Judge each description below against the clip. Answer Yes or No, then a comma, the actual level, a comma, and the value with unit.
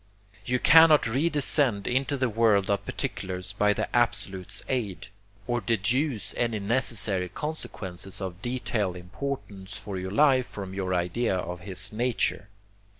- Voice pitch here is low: Yes, low, 105 Hz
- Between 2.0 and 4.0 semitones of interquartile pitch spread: No, average, 4.9 semitones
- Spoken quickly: No, slow, 135 wpm